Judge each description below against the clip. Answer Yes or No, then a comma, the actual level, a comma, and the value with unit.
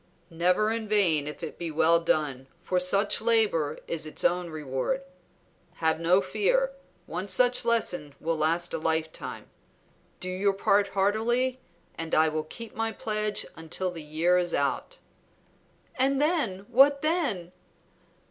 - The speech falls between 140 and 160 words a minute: Yes, average, 145 wpm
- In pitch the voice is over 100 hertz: Yes, medium, 185 Hz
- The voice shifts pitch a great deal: Yes, wide, 5.7 semitones